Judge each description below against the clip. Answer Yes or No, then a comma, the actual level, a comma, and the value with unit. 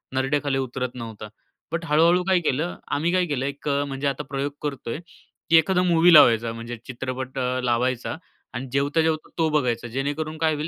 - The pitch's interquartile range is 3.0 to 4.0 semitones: Yes, average, 3.7 semitones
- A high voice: No, medium, 140 Hz